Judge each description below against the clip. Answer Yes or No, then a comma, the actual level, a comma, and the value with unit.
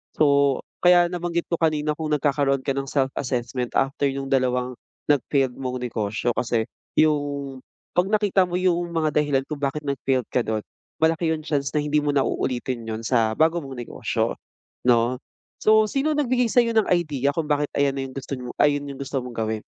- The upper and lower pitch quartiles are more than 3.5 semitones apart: Yes, average, 3.9 semitones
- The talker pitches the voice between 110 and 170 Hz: Yes, medium, 140 Hz